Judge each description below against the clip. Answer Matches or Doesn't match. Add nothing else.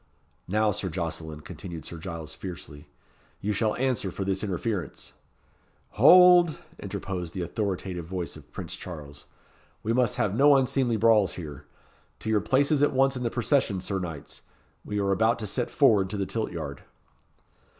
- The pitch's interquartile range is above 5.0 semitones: Matches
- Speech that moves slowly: Doesn't match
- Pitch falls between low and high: Doesn't match